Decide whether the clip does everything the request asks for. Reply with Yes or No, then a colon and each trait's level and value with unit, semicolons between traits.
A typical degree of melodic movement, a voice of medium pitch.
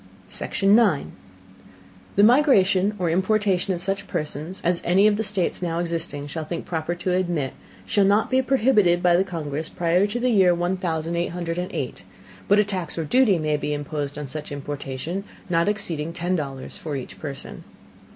Yes: average, 4.0 semitones; medium, 175 Hz